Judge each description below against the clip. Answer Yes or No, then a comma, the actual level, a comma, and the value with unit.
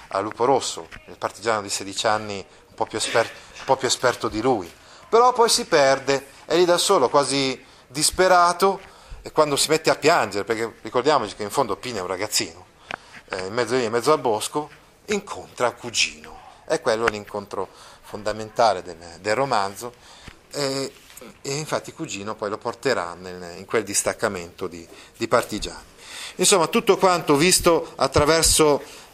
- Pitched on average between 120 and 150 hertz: Yes, low, 130 Hz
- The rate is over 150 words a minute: Yes, average, 160 wpm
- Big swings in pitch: Yes, wide, 6.7 semitones